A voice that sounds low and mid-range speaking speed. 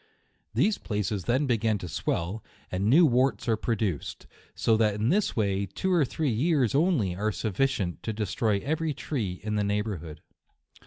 Yes: low, 110 Hz; average, 170 wpm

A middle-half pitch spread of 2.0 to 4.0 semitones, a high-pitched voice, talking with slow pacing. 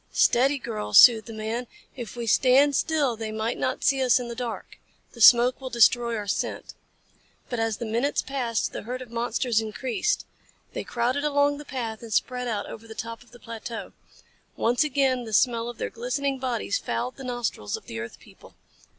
No: narrow, 2.4 semitones; high, 240 Hz; average, 195 wpm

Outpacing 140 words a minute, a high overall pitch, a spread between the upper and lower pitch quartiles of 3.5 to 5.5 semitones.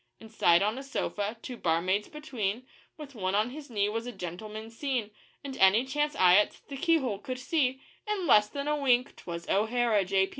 Yes: average, 190 wpm; high, 230 Hz; average, 5.0 semitones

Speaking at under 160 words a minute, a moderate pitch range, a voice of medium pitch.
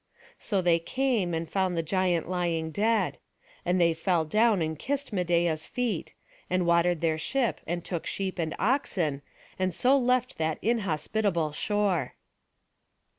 Yes: average, 145 wpm; average, 4.2 semitones; medium, 180 Hz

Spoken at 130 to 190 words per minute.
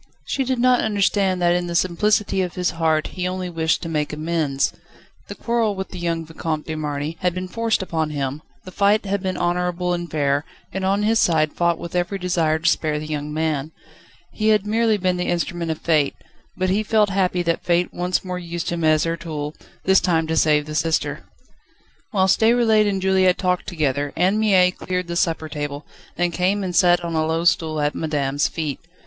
No: fast, 205 wpm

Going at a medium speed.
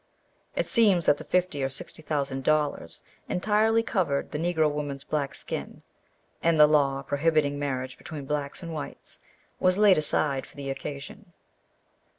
Yes: average, 155 wpm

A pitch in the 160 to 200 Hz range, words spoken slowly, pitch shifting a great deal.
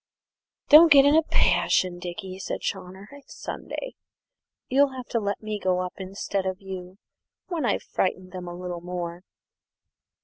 No: high, 190 Hz; average, 160 wpm; wide, 5.7 semitones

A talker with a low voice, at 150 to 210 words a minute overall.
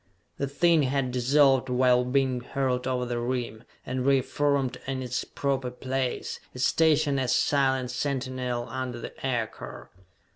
No: low, 130 Hz; average, 140 wpm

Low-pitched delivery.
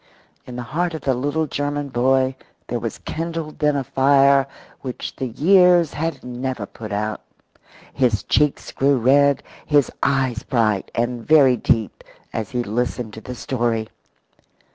Yes: low, 130 Hz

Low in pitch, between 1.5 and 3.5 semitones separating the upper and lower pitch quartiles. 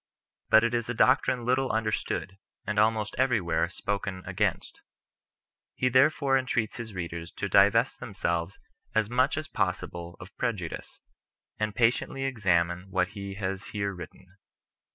No: low, 105 Hz; average, 4.7 semitones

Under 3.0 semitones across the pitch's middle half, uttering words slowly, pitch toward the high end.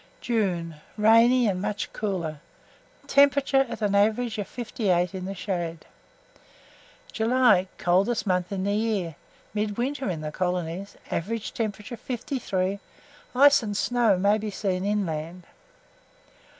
No: average, 3.9 semitones; slow, 125 wpm; high, 205 Hz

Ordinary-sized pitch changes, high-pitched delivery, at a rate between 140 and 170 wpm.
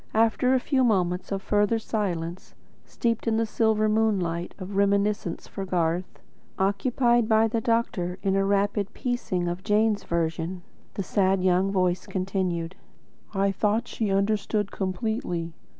Yes: average, 3.1 semitones; high, 200 Hz; average, 145 wpm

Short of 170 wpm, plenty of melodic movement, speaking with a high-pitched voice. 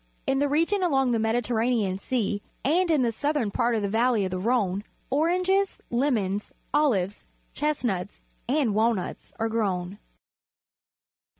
Yes: slow, 135 wpm; wide, 5.9 semitones; high, 235 Hz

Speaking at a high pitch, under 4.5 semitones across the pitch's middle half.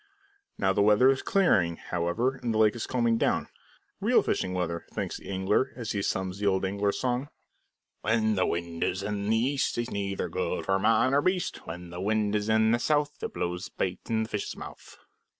No: low, 105 Hz; average, 3.8 semitones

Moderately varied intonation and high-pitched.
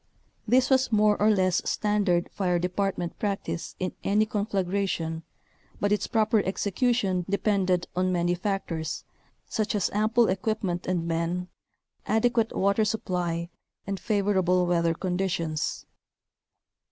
Yes: average, 3.0 semitones; high, 195 Hz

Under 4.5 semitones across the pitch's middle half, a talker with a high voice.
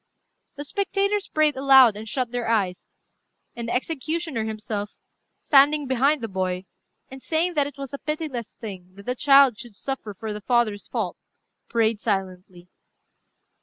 No: average, 5.2 semitones; high, 245 Hz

